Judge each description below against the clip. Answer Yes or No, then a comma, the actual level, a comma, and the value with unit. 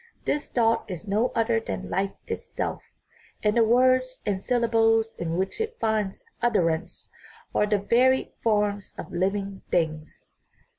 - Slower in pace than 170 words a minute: Yes, average, 145 wpm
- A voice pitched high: Yes, high, 215 Hz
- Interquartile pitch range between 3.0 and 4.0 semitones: Yes, average, 3.5 semitones